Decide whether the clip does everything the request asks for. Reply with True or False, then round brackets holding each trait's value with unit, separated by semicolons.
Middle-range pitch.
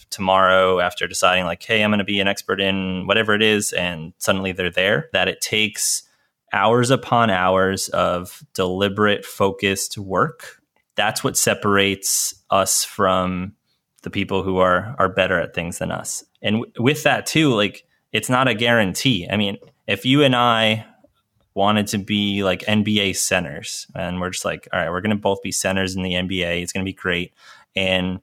False (100 Hz)